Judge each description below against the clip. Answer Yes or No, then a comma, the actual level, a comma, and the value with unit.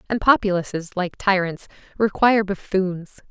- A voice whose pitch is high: Yes, high, 195 Hz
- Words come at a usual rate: No, slow, 110 wpm